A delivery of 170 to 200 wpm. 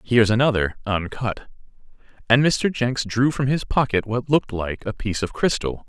Yes: average, 175 wpm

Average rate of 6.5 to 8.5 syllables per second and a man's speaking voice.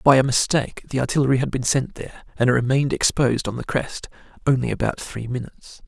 Yes: 6.6 syllables/s; male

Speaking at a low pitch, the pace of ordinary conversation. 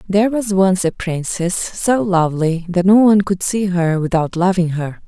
No: medium, 185 Hz; average, 190 wpm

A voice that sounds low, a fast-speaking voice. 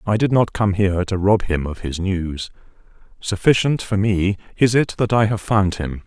Yes: low, 100 Hz; fast, 210 wpm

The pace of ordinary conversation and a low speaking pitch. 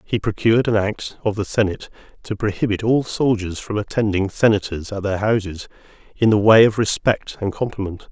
Yes: average, 175 wpm; low, 105 Hz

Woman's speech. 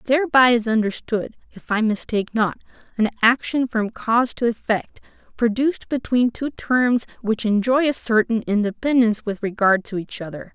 Yes: female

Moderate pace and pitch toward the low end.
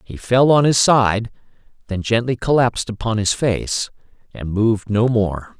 Yes: average, 160 wpm; low, 115 Hz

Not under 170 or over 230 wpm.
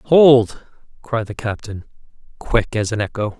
No: average, 140 wpm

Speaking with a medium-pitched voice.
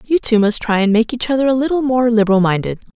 No: high, 230 Hz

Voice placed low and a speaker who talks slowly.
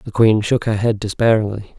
No: low, 110 Hz; average, 200 wpm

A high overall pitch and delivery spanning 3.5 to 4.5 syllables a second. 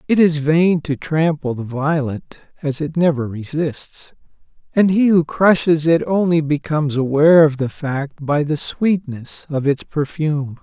No: medium, 150 Hz; 4.2 syllables/s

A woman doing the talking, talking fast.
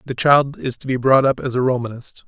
No: male; fast, 265 wpm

